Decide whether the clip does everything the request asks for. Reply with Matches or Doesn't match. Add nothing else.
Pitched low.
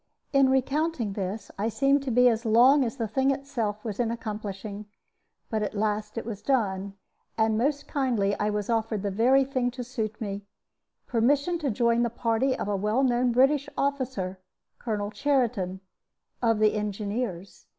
Doesn't match